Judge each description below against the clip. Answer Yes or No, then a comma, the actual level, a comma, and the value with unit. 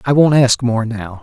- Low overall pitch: Yes, low, 125 Hz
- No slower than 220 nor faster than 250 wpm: Yes, fast, 245 wpm